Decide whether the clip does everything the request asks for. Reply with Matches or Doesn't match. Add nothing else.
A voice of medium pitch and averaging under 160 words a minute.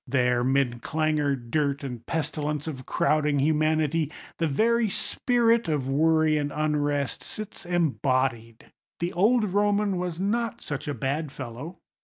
Matches